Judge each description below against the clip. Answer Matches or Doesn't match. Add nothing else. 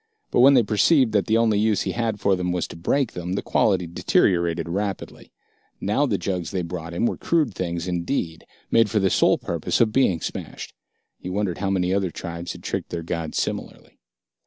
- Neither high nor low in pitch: Doesn't match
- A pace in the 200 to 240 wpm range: Matches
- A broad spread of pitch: Doesn't match